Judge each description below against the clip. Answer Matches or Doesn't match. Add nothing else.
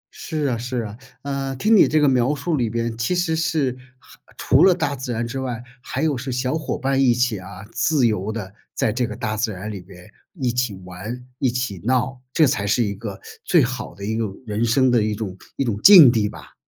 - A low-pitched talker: Matches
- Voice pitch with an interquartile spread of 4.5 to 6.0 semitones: Doesn't match